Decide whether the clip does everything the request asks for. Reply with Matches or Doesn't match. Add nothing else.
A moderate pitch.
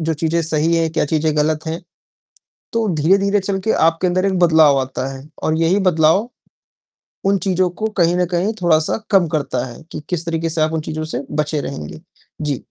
Matches